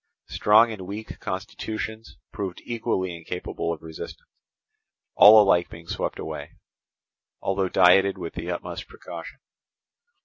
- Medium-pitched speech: No, very low, 95 Hz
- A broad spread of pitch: No, average, 3.4 semitones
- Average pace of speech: No, slow, 115 wpm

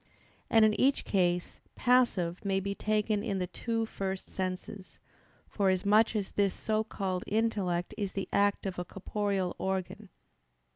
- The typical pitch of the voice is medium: No, high, 200 Hz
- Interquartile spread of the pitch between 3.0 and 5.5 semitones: No, narrow, 2.4 semitones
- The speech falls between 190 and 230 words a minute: No, average, 145 wpm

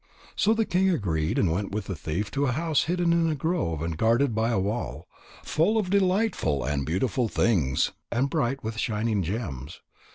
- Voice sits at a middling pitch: No, low, 115 Hz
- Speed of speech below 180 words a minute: No, average, 190 wpm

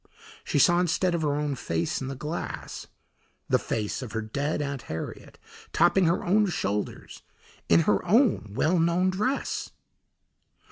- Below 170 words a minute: Yes, average, 150 wpm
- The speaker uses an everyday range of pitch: No, wide, 7.1 semitones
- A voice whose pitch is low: No, medium, 150 Hz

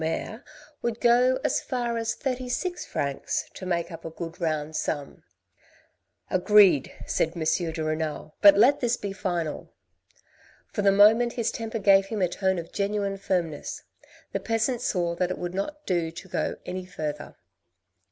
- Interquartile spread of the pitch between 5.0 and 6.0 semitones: Yes, average, 5.3 semitones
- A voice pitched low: No, high, 190 Hz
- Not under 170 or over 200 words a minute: Yes, average, 180 wpm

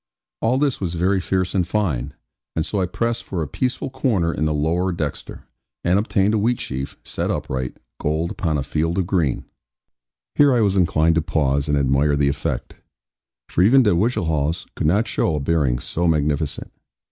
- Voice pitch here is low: Yes, very low, 85 Hz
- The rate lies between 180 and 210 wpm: Yes, average, 185 wpm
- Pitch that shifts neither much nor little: Yes, average, 5.0 semitones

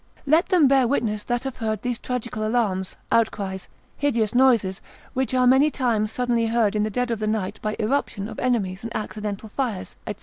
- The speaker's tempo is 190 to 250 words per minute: Yes, average, 195 wpm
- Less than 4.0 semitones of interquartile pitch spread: Yes, average, 3.0 semitones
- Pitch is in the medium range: No, high, 230 Hz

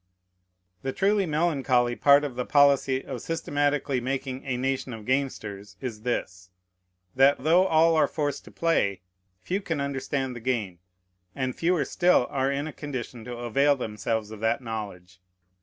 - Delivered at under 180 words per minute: Yes, average, 155 wpm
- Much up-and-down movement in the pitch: No, average, 3.6 semitones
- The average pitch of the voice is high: No, low, 130 Hz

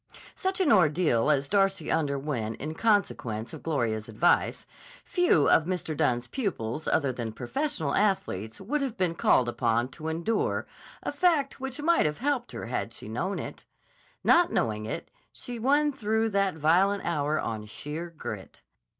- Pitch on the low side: No, medium, 160 Hz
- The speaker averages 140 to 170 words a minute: Yes, average, 160 wpm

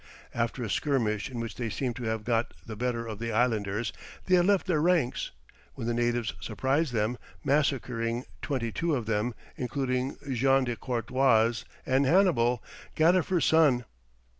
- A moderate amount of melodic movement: Yes, average, 3.2 semitones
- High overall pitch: No, low, 125 Hz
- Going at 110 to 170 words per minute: Yes, average, 160 wpm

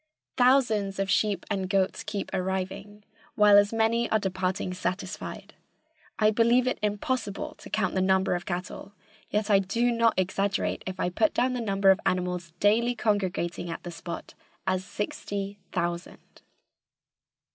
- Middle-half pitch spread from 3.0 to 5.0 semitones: No, narrow, 2.6 semitones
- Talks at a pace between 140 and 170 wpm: Yes, average, 155 wpm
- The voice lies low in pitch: No, high, 200 Hz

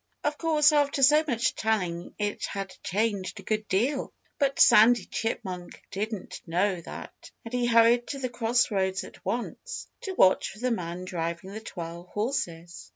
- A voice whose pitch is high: Yes, high, 215 Hz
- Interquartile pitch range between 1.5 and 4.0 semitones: No, average, 4.9 semitones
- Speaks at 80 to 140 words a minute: No, average, 165 wpm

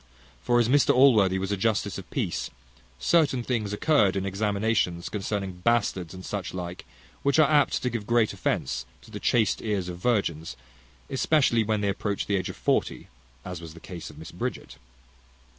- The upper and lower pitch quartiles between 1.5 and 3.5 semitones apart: No, average, 4.3 semitones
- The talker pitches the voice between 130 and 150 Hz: No, low, 100 Hz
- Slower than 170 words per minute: No, average, 180 wpm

